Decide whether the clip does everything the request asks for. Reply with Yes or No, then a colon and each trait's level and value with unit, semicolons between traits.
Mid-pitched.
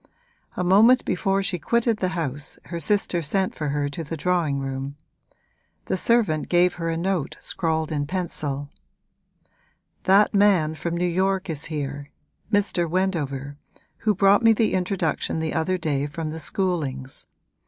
Yes: medium, 170 Hz